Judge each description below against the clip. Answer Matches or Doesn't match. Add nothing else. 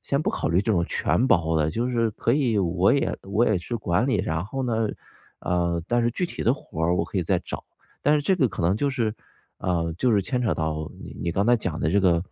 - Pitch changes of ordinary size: Doesn't match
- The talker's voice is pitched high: Doesn't match